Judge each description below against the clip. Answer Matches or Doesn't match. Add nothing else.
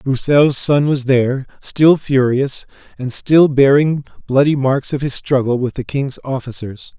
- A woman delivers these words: Doesn't match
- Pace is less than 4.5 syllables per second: Matches